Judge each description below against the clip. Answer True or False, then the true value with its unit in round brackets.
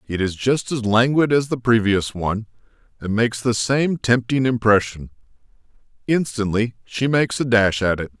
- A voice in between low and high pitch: False (115 Hz)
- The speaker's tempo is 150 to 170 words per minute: True (160 wpm)